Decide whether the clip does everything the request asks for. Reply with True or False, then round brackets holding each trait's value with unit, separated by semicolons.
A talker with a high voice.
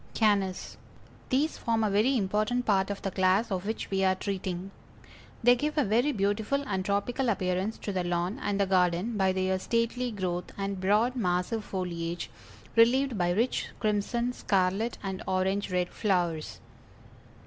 True (200 Hz)